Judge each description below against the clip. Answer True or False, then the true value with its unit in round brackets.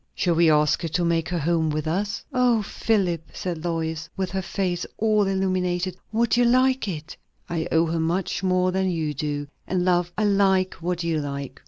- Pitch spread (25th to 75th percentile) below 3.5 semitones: True (2.9 semitones)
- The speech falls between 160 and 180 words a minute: False (195 wpm)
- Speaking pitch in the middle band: True (175 Hz)